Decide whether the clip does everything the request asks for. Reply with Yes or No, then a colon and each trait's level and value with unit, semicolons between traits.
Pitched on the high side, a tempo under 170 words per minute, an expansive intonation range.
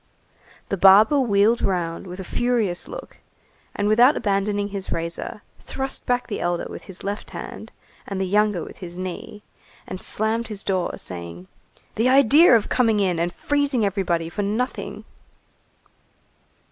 No: high, 205 Hz; average, 150 wpm; average, 4.2 semitones